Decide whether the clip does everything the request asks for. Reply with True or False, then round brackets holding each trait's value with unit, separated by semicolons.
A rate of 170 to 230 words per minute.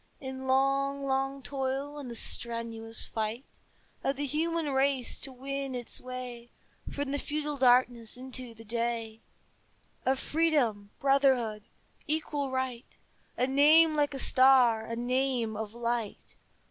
False (135 wpm)